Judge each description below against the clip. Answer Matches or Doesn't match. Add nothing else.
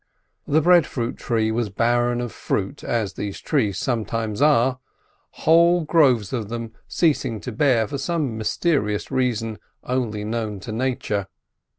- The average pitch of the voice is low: Matches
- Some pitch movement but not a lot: Matches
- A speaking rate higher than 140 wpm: Doesn't match